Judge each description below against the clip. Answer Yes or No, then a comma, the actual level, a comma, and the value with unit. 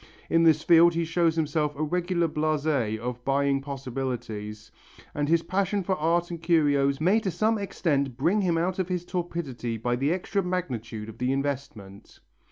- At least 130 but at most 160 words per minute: No, average, 175 wpm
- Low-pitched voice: No, medium, 155 Hz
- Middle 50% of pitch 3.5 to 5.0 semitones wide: Yes, average, 4.5 semitones